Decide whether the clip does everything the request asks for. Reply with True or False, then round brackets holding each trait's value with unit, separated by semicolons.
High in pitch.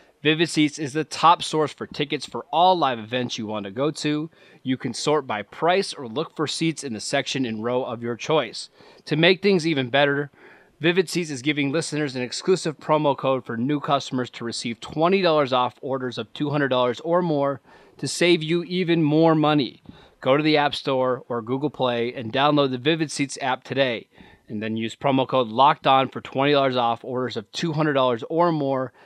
False (140 Hz)